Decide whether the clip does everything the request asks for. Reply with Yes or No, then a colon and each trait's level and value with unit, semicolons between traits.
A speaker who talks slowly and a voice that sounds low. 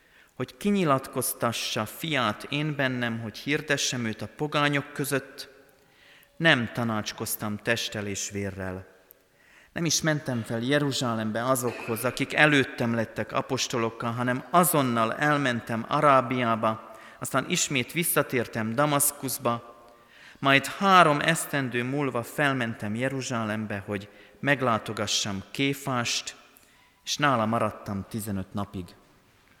Yes: slow, 95 wpm; low, 120 Hz